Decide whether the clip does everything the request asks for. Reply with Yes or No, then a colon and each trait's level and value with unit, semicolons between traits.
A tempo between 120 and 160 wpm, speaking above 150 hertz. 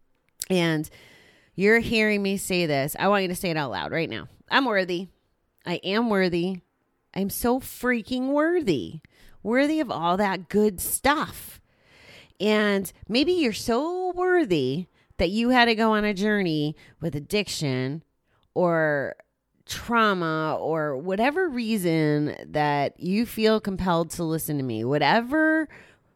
Yes: average, 140 wpm; high, 190 Hz